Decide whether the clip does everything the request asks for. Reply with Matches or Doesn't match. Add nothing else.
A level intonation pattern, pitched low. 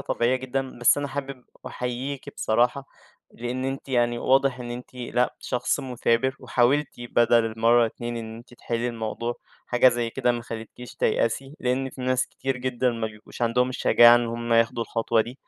Matches